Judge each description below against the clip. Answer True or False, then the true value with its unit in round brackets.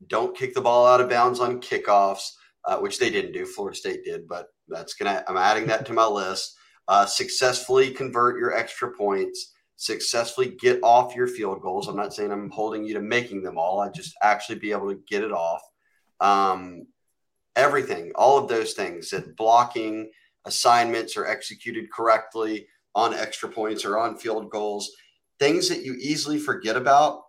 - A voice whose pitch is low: True (125 Hz)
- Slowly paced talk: False (185 wpm)